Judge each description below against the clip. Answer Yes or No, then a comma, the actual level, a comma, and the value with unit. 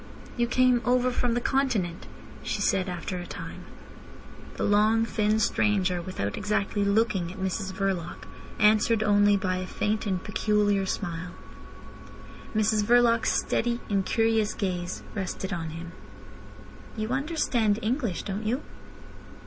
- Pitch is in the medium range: No, high, 210 Hz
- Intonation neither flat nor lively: Yes, average, 3.3 semitones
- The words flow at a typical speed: No, slow, 130 wpm